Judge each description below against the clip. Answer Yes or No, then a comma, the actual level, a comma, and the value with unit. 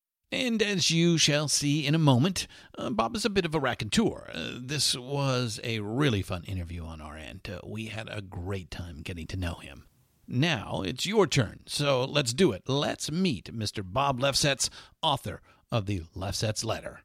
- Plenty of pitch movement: Yes, wide, 7.0 semitones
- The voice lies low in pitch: Yes, low, 120 Hz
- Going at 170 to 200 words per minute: Yes, average, 190 wpm